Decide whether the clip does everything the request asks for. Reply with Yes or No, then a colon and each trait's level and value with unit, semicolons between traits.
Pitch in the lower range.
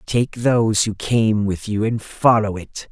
Yes: low, 110 Hz